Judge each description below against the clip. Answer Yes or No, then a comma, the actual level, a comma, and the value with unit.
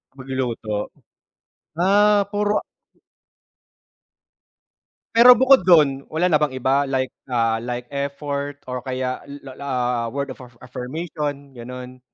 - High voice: No, low, 135 Hz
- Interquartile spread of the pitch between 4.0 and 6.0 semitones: No, average, 3.5 semitones